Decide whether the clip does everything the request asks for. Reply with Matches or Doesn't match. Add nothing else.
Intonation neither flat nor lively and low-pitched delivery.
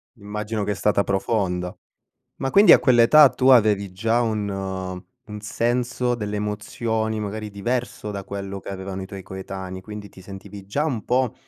Matches